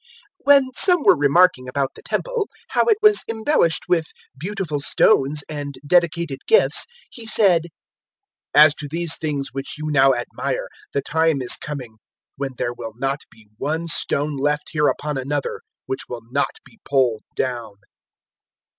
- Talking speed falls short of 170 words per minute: Yes, average, 160 wpm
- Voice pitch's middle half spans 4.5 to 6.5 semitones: No, average, 4.1 semitones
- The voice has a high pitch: No, medium, 150 Hz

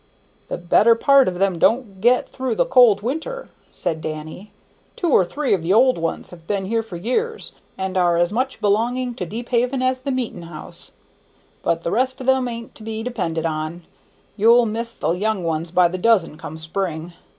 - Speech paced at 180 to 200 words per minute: Yes, average, 195 wpm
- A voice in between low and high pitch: No, high, 215 Hz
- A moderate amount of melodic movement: No, wide, 6.3 semitones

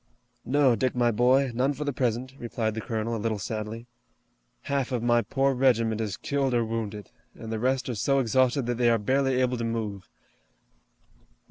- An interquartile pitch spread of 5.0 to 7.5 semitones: No, average, 2.7 semitones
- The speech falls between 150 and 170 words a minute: No, average, 190 wpm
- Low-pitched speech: Yes, low, 120 Hz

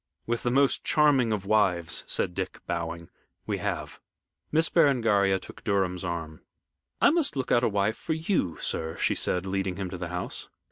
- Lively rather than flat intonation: Yes, wide, 6.2 semitones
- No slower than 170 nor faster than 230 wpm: Yes, average, 180 wpm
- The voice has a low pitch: Yes, low, 100 Hz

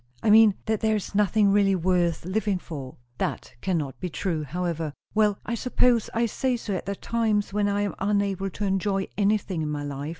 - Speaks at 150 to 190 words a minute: No, average, 200 wpm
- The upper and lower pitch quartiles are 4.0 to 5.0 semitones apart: No, average, 3.2 semitones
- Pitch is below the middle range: No, high, 200 Hz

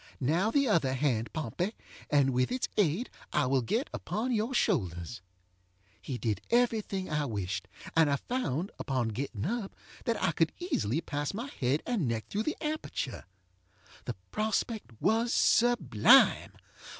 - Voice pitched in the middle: Yes, medium, 150 Hz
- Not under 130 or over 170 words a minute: Yes, average, 150 wpm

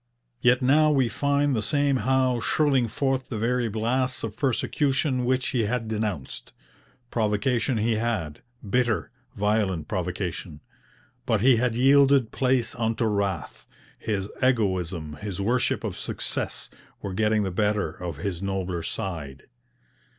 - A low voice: Yes, low, 110 Hz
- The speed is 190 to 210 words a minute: No, slow, 135 wpm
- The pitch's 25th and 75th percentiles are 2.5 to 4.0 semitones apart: No, average, 4.7 semitones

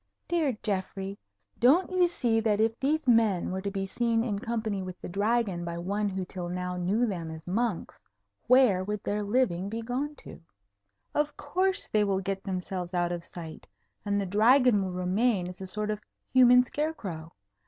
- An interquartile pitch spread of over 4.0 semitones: Yes, average, 4.7 semitones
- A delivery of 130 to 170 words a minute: No, average, 185 wpm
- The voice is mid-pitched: No, high, 205 Hz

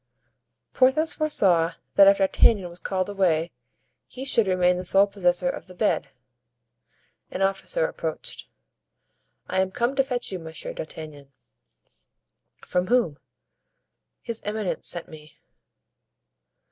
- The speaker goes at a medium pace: No, slow, 120 wpm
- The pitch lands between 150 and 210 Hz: Yes, high, 190 Hz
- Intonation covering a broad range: No, average, 5.0 semitones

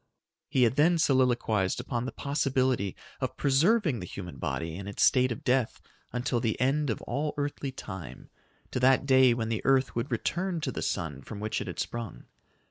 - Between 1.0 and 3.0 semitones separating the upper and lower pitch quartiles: No, average, 3.9 semitones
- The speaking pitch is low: Yes, low, 125 Hz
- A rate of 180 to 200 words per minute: Yes, average, 195 wpm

